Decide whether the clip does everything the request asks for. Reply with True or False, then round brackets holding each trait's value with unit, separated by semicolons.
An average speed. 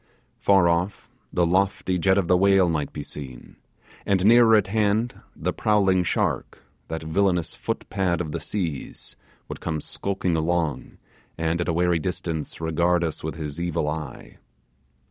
True (155 wpm)